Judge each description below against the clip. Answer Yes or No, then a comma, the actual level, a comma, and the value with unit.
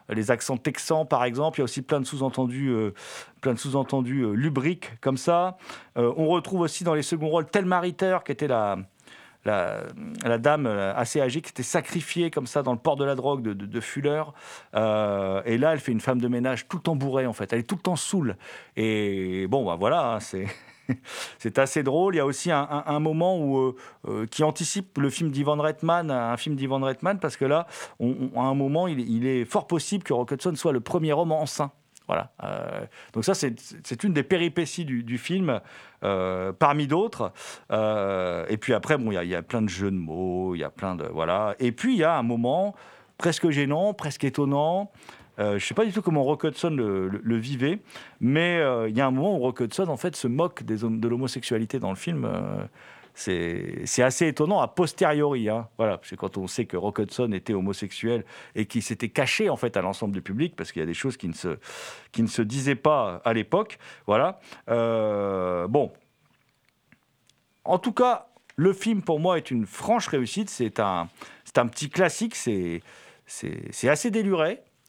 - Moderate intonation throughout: No, wide, 6.0 semitones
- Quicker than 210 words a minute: Yes, fast, 220 wpm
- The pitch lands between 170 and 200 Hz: No, low, 135 Hz